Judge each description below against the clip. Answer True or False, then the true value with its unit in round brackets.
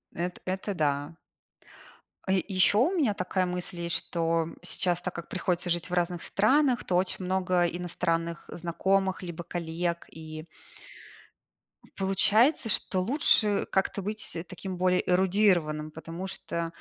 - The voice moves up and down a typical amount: False (2.1 semitones)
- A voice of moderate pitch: True (180 Hz)